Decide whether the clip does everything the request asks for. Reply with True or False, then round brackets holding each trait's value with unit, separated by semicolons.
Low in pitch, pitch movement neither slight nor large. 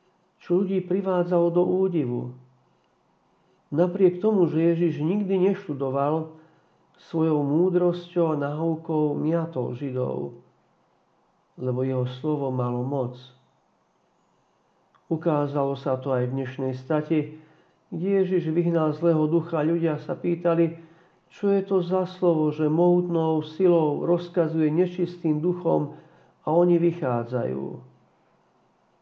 False (165 Hz; 3.2 semitones)